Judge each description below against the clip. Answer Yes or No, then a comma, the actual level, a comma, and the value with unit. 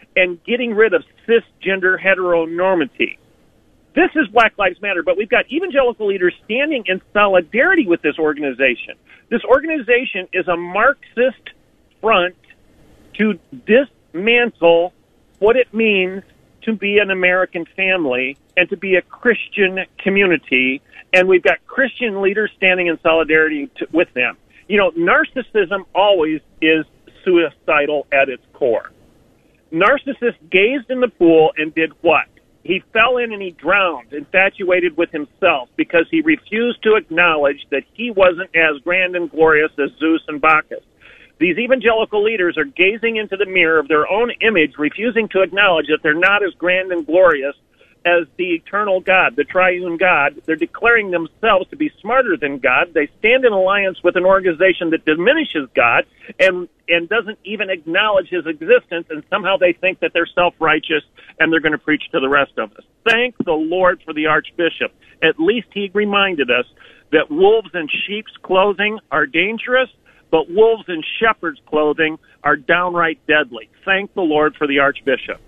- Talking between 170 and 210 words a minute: No, average, 160 wpm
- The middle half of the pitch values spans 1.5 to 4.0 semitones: No, wide, 5.5 semitones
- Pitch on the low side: No, medium, 185 Hz